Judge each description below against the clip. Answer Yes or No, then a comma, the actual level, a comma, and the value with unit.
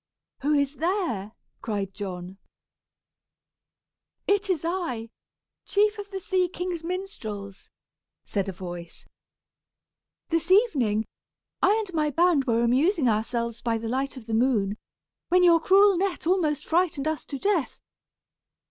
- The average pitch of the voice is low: No, very high, 295 Hz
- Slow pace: Yes, slow, 130 wpm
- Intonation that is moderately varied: No, wide, 8.3 semitones